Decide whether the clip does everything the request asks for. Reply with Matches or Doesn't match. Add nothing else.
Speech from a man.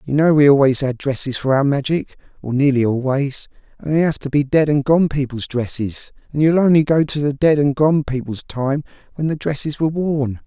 Matches